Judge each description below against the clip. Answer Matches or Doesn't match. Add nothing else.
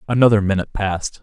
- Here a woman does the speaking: Doesn't match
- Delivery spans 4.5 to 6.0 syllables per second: Doesn't match